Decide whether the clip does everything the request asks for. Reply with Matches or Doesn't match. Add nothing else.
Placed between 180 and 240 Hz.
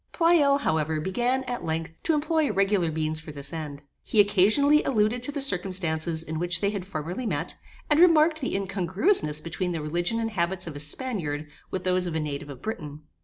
Matches